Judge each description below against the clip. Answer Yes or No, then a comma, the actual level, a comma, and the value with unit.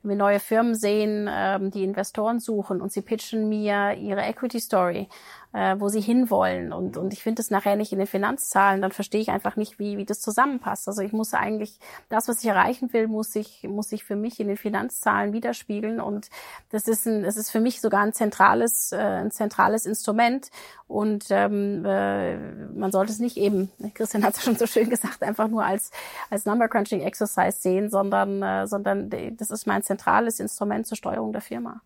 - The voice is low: No, high, 210 Hz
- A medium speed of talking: No, fast, 200 wpm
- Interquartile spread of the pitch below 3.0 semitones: Yes, narrow, 2.4 semitones